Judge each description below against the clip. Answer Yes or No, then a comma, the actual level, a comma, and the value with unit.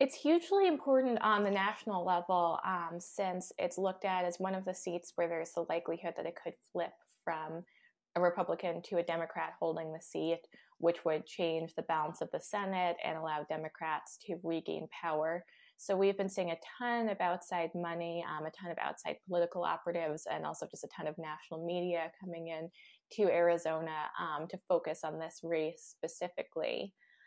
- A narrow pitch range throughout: Yes, narrow, 2.3 semitones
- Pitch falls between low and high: Yes, medium, 170 Hz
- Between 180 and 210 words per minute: Yes, average, 185 wpm